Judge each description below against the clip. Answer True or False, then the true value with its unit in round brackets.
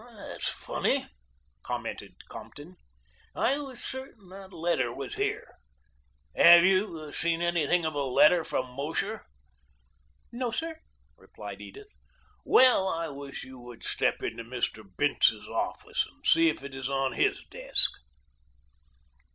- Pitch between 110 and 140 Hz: False (165 Hz)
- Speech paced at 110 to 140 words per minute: True (135 wpm)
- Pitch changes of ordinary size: False (6.0 semitones)